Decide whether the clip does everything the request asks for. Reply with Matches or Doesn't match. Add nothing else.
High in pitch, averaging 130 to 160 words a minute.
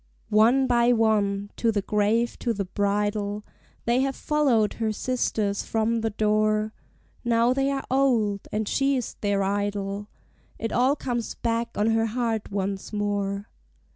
Matches